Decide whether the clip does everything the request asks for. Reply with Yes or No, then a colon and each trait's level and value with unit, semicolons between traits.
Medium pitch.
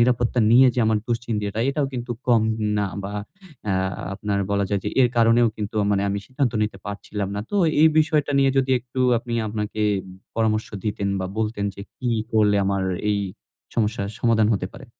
No: low, 110 Hz